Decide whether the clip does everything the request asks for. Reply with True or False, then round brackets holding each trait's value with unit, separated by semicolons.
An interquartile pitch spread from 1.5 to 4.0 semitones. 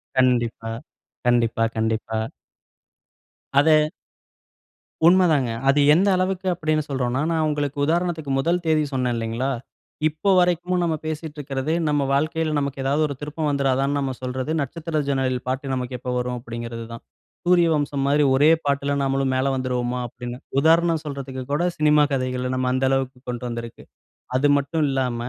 True (3.5 semitones)